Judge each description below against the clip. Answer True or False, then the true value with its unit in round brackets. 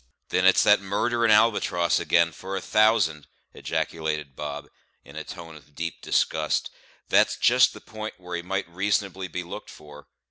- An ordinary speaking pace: True (165 wpm)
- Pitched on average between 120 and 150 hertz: False (90 Hz)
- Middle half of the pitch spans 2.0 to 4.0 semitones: False (4.5 semitones)